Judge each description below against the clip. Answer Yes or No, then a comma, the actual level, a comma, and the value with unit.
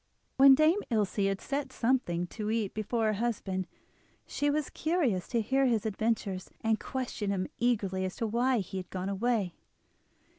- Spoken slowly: No, average, 170 wpm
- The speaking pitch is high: Yes, high, 220 Hz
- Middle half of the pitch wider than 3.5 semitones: Yes, average, 4.7 semitones